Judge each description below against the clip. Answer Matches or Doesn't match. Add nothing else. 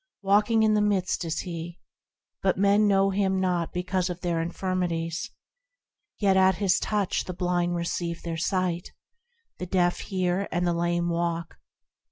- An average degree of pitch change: Doesn't match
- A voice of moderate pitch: Matches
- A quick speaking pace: Doesn't match